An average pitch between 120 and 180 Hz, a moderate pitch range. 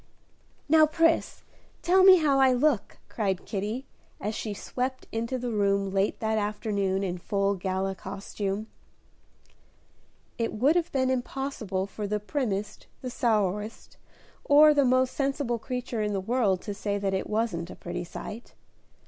No: high, 215 Hz; average, 4.6 semitones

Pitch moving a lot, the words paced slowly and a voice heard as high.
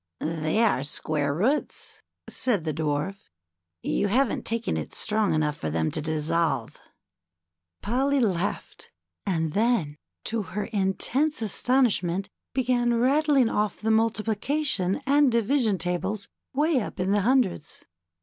Yes: wide, 6.7 semitones; slow, 125 wpm; high, 210 Hz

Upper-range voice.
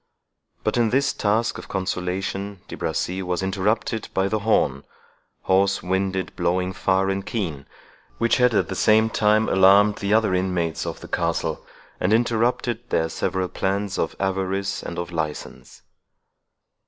No: very low, 95 Hz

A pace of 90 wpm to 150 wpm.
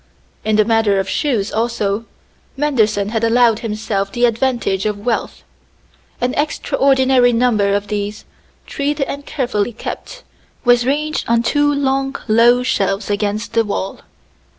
Yes: slow, 135 wpm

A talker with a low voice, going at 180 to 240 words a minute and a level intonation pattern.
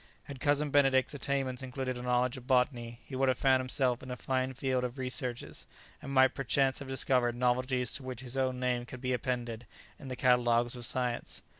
Yes: low, 130 Hz; average, 200 wpm; narrow, 1.2 semitones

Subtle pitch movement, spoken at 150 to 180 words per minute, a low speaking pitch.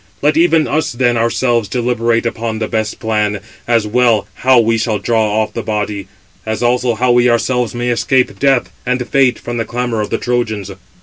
No: narrow, 2.1 semitones; average, 190 wpm; low, 120 Hz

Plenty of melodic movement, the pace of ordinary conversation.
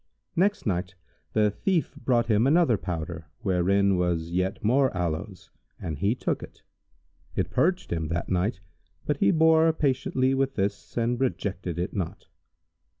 Yes: wide, 6.9 semitones; average, 150 wpm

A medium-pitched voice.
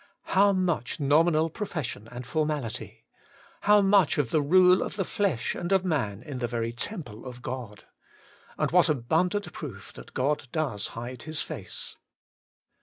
Yes: medium, 150 Hz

